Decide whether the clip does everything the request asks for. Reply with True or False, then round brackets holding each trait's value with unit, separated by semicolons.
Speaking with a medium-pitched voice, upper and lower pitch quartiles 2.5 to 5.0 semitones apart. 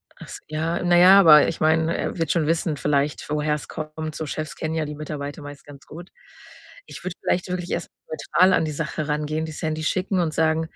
False (155 Hz; 1.8 semitones)